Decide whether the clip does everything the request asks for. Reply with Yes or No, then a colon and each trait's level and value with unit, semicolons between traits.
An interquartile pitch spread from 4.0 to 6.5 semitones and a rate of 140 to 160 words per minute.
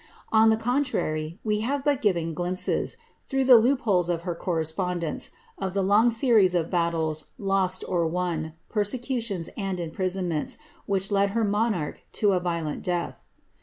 Yes: average, 4.5 semitones; average, 150 wpm